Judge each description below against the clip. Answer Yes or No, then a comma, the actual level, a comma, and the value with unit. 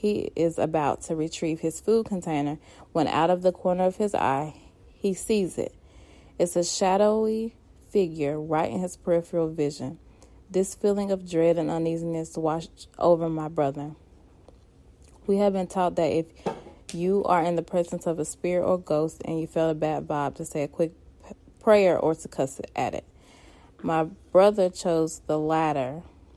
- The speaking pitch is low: No, medium, 165 Hz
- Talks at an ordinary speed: Yes, average, 170 wpm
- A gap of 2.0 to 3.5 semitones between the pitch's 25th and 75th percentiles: Yes, average, 3.0 semitones